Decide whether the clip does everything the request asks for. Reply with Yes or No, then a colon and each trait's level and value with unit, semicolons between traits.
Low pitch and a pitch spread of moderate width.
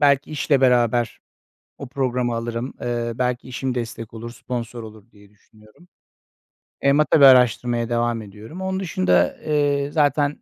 Yes: low, 120 Hz; average, 3.3 semitones